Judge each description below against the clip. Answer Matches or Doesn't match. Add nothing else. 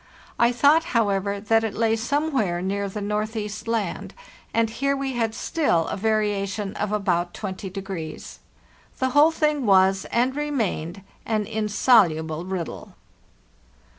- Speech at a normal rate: Doesn't match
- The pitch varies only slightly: Doesn't match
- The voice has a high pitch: Matches